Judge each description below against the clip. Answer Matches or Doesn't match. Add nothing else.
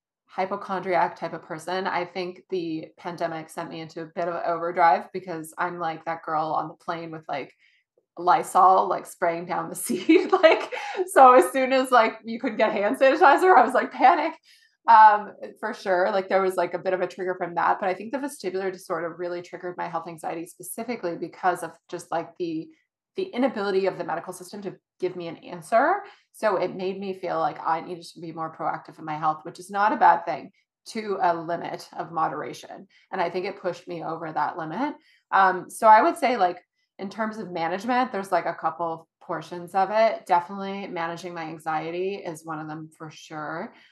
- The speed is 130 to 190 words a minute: Doesn't match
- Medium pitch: Matches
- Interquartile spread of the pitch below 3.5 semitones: Doesn't match